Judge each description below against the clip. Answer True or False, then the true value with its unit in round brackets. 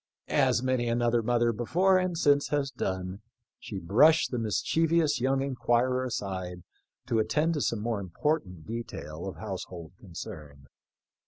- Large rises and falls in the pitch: True (6.4 semitones)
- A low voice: True (120 Hz)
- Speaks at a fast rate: False (145 wpm)